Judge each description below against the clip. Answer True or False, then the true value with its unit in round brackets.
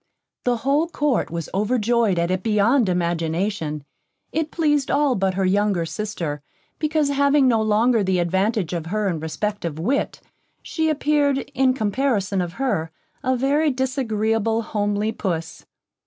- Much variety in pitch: True (6.3 semitones)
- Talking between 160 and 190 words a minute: False (145 wpm)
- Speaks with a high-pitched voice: True (215 Hz)